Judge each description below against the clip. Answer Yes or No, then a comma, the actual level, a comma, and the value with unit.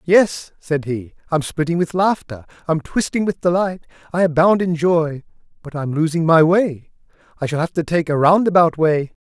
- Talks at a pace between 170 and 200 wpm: Yes, average, 180 wpm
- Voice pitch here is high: No, medium, 165 Hz